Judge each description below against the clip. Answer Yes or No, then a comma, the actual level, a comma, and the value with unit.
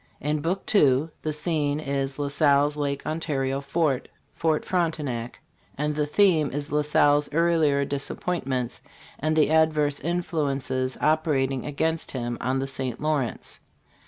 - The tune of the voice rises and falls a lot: No, narrow, 2.5 semitones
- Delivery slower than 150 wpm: Yes, slow, 135 wpm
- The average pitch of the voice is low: No, medium, 145 Hz